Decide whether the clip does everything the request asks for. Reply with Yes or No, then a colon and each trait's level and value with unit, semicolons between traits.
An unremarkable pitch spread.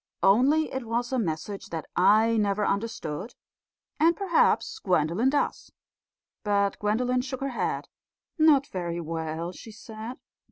No: wide, 5.9 semitones